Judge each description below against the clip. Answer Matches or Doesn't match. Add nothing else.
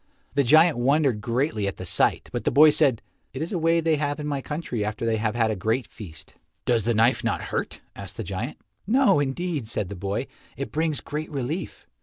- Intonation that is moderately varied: Doesn't match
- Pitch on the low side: Matches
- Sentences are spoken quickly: Matches